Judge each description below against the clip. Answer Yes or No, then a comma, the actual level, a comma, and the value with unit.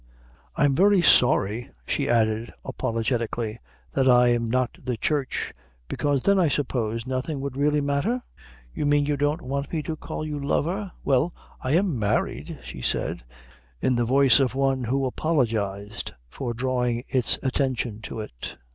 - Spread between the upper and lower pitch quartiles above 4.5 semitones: No, average, 3.6 semitones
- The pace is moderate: Yes, average, 155 wpm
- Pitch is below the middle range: Yes, low, 130 Hz